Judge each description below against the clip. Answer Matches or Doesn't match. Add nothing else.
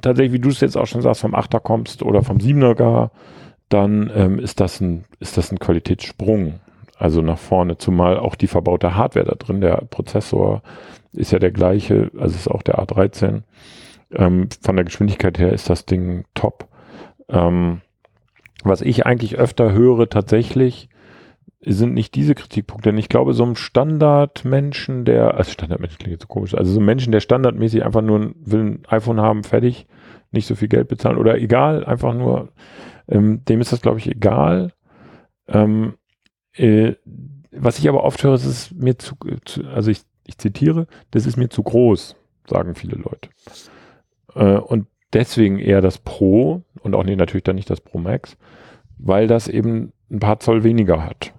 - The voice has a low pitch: Matches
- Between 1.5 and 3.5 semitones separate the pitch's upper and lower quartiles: Doesn't match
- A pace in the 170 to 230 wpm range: Matches